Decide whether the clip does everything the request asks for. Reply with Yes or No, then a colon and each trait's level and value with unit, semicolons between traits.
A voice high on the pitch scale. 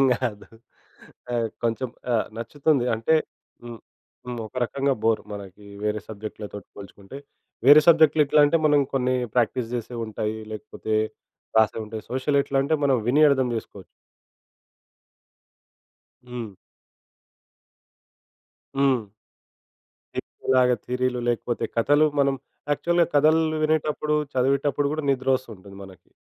No: low, 125 Hz